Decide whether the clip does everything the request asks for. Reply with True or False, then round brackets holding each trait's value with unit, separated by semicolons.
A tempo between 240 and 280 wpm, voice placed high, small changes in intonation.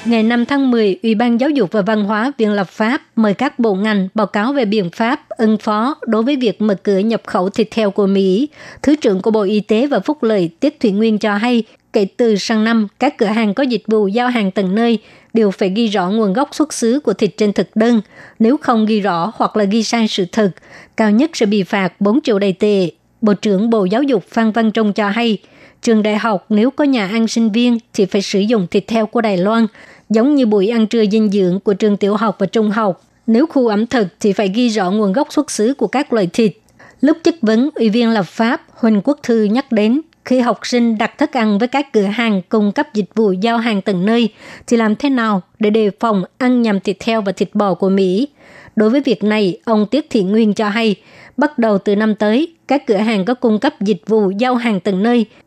True (245 wpm; 220 Hz; 2.3 semitones)